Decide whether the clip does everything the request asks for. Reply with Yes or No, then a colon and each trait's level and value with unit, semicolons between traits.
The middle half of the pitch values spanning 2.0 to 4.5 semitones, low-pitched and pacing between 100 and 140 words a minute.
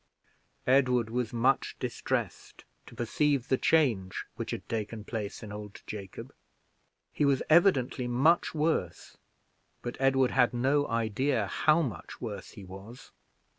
Yes: average, 4.2 semitones; low, 125 Hz; slow, 135 wpm